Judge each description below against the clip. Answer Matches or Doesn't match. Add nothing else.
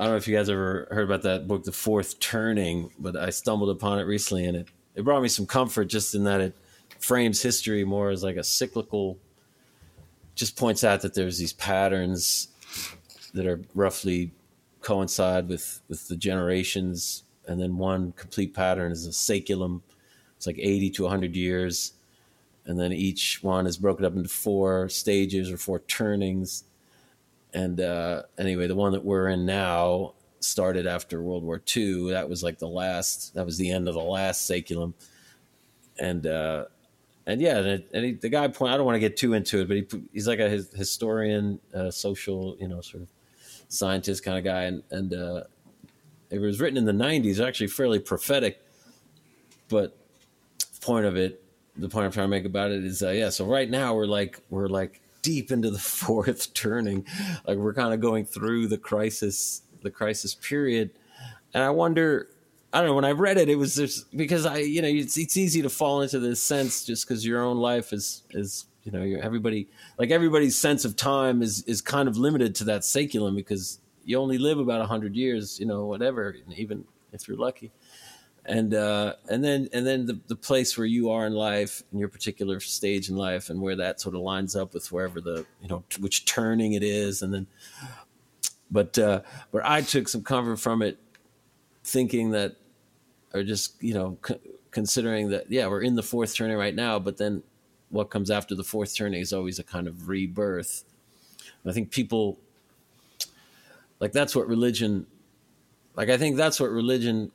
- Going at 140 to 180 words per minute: Doesn't match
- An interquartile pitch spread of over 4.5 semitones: Doesn't match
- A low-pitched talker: Matches